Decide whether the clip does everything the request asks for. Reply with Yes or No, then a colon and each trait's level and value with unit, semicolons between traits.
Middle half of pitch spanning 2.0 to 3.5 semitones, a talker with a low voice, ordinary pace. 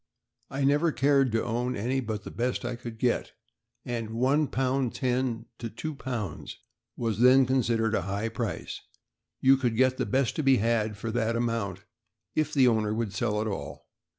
Yes: average, 2.9 semitones; low, 120 Hz; average, 175 wpm